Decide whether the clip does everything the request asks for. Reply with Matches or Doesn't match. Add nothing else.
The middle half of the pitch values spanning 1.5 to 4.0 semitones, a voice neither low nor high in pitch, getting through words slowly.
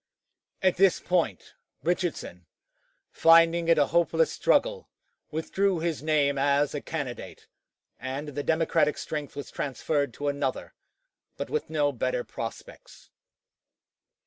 Matches